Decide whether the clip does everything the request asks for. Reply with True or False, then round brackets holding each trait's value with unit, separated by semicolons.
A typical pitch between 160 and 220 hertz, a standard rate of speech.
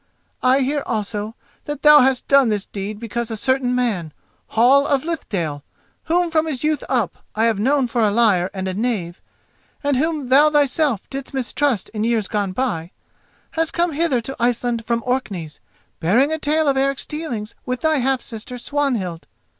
False (250 Hz; 170 wpm)